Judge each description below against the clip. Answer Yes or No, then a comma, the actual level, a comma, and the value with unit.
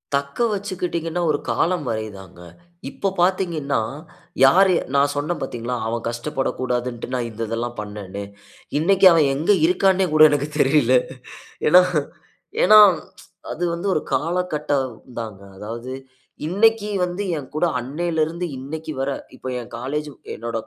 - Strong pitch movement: Yes, wide, 6.4 semitones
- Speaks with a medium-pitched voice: Yes, medium, 150 Hz